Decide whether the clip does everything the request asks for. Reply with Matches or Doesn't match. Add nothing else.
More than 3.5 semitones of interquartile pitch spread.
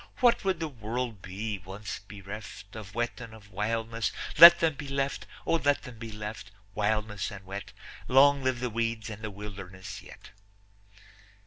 Matches